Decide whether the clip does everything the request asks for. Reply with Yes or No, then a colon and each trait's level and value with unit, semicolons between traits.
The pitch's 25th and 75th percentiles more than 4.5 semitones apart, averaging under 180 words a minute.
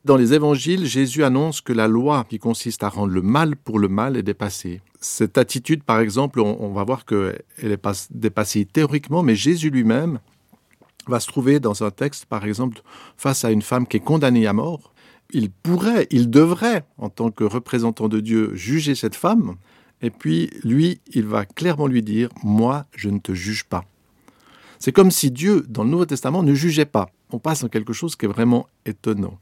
No: average, 5.2 semitones; average, 200 wpm